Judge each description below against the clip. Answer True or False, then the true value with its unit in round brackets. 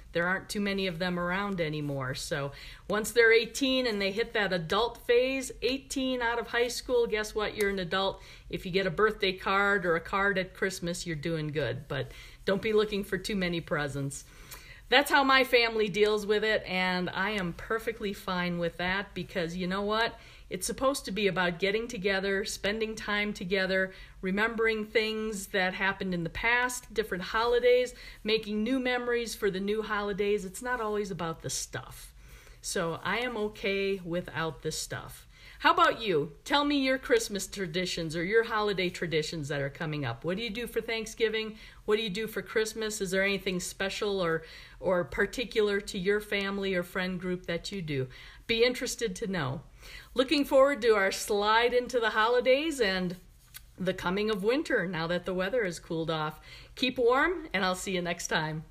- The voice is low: False (200 Hz)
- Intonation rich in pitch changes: False (3.8 semitones)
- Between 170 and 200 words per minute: True (185 wpm)